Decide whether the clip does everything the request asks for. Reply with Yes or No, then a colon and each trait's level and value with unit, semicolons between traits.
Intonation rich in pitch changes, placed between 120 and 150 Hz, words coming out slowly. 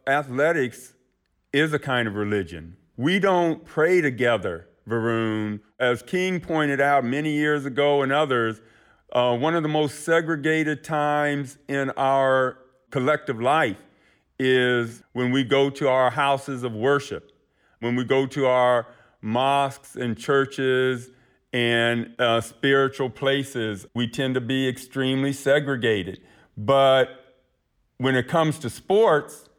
No: narrow, 2.6 semitones; low, 130 Hz; slow, 130 wpm